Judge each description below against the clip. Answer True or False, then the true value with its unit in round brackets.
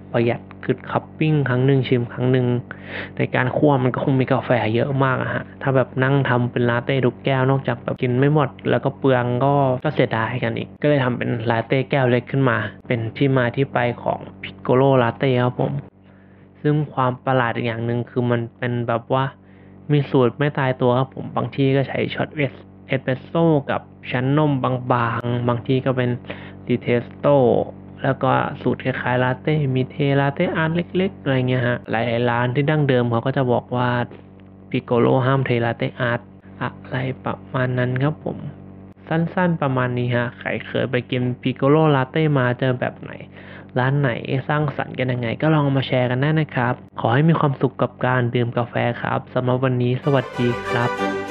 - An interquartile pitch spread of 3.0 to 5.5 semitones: False (2.4 semitones)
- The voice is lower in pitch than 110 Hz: False (125 Hz)